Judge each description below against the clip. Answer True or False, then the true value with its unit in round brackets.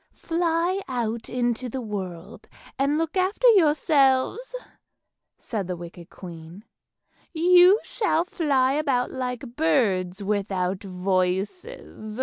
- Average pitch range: False (8.8 semitones)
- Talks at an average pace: False (110 wpm)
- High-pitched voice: True (250 Hz)